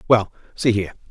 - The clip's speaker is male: Yes, male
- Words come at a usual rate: Yes, average, 165 wpm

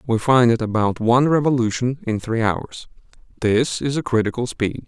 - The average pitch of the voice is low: Yes, low, 120 Hz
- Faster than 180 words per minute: No, average, 170 wpm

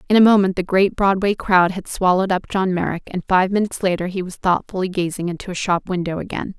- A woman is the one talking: Yes, female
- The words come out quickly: Yes, fast, 230 wpm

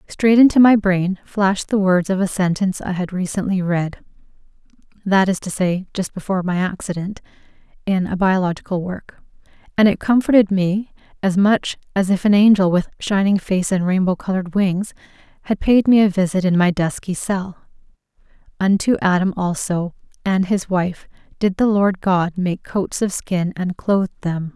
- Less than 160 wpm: No, average, 165 wpm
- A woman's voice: Yes, female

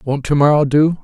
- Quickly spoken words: No, average, 175 wpm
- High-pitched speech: No, medium, 145 Hz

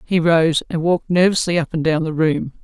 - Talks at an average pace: No, fast, 230 wpm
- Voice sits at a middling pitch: Yes, medium, 165 Hz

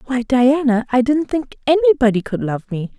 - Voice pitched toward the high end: Yes, very high, 255 Hz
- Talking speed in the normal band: Yes, average, 180 wpm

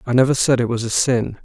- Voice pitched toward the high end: No, low, 125 Hz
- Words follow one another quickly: Yes, fast, 290 wpm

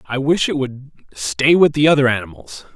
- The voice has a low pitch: Yes, low, 130 Hz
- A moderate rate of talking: Yes, average, 195 wpm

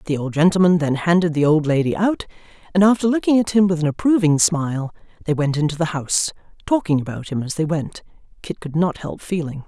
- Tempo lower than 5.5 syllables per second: No, 6.0 syllables/s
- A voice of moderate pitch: Yes, medium, 165 Hz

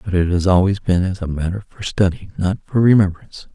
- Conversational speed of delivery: No, fast, 220 wpm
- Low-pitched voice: Yes, very low, 95 Hz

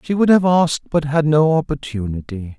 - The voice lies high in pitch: No, medium, 150 Hz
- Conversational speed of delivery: Yes, average, 185 wpm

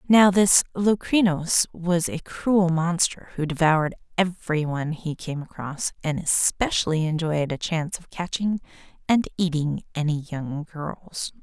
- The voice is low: No, medium, 165 Hz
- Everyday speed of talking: No, slow, 130 wpm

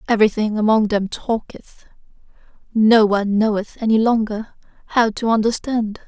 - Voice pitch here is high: Yes, high, 220 Hz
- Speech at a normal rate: No, slow, 120 wpm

